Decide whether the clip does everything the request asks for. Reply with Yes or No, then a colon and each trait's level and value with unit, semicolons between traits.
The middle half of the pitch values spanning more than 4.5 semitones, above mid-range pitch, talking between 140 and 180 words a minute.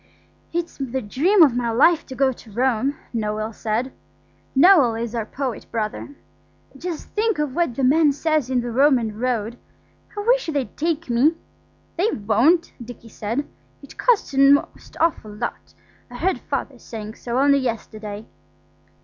Yes: average, 5.1 semitones; very high, 260 Hz; average, 160 wpm